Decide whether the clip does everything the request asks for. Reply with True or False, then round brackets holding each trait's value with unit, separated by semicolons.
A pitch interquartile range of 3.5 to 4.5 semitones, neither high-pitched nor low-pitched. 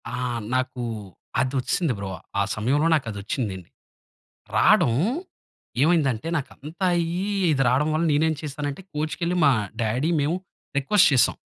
True (4.1 semitones; 145 Hz)